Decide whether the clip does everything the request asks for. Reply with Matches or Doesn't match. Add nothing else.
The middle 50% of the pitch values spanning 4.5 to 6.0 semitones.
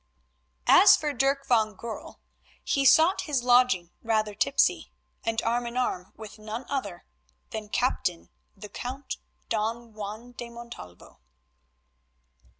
Doesn't match